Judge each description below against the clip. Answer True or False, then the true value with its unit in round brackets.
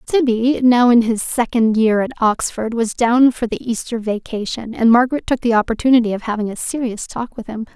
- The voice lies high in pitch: True (235 Hz)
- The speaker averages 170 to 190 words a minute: False (200 wpm)